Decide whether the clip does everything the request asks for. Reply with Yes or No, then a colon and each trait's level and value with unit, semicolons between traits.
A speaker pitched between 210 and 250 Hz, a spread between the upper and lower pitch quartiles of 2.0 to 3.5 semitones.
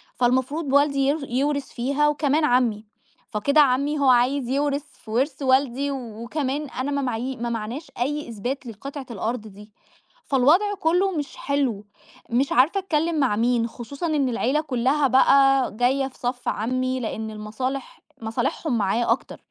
No: very high, 265 Hz; average, 3.0 semitones